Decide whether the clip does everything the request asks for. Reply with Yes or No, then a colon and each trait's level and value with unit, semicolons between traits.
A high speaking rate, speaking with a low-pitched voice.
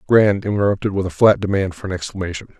Yes: fast, 210 wpm; very low, 95 Hz